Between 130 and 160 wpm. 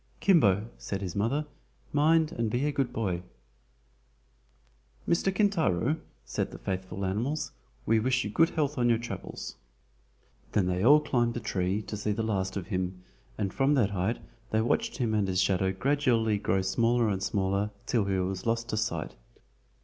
No: average, 170 wpm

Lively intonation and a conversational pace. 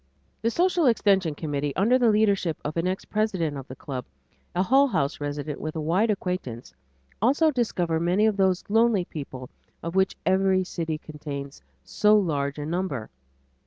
Yes: wide, 6.0 semitones; average, 165 wpm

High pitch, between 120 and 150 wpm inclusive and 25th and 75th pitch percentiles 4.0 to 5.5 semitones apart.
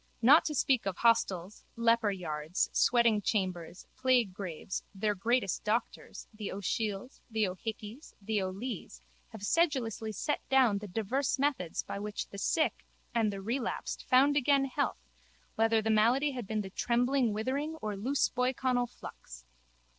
Yes: high, 225 Hz; average, 140 wpm; average, 4.4 semitones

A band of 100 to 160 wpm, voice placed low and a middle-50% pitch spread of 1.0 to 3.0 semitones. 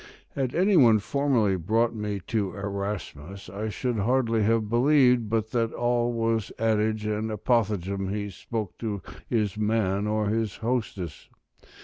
Yes: average, 140 wpm; low, 110 Hz; narrow, 2.5 semitones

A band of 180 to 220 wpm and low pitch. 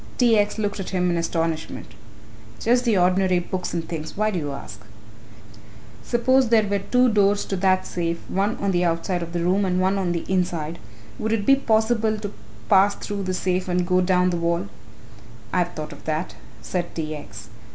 No: average, 200 wpm; medium, 185 Hz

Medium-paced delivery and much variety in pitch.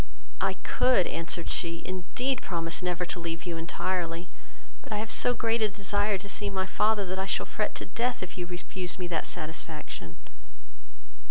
No: average, 180 wpm; average, 3.4 semitones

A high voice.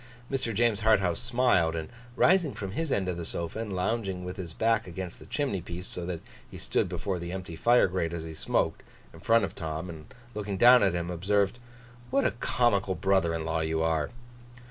No: very low, 95 Hz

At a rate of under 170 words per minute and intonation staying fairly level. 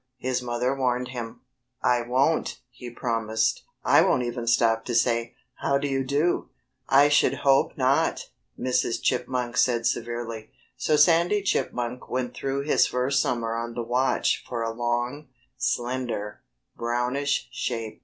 Yes: average, 145 wpm; narrow, 2.2 semitones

